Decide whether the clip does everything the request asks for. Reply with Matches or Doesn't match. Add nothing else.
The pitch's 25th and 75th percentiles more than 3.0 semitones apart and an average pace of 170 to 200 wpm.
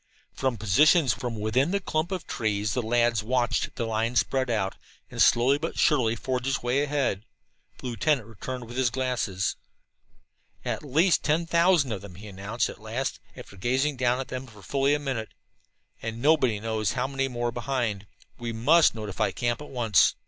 Matches